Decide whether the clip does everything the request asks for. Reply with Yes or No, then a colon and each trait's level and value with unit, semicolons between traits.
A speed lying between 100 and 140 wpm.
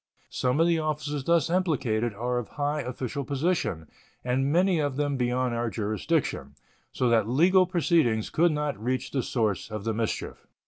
No: average, 170 wpm